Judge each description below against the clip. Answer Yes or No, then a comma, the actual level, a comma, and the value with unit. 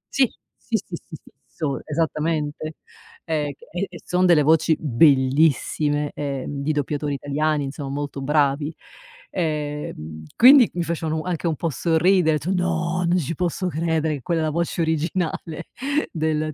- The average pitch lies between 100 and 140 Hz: No, medium, 155 Hz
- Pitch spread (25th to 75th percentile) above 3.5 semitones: No, narrow, 2.5 semitones